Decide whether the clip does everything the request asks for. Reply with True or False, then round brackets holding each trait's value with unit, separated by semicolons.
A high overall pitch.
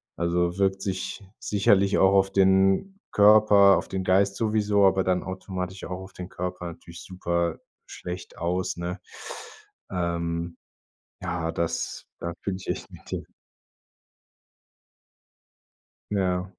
False (95 Hz)